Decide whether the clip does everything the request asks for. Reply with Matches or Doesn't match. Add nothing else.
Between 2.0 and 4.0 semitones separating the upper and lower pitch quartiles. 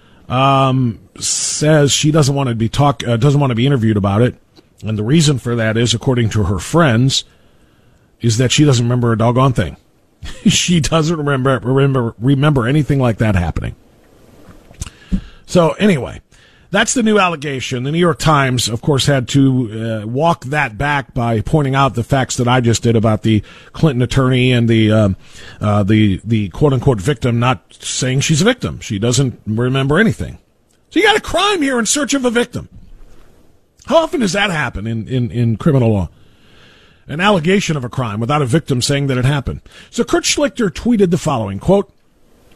Doesn't match